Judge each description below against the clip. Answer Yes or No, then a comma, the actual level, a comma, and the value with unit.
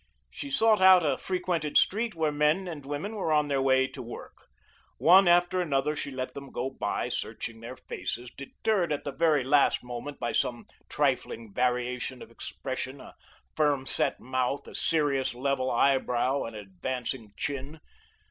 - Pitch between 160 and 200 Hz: No, medium, 140 Hz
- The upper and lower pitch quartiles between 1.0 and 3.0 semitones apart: No, average, 4.0 semitones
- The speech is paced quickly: No, average, 165 wpm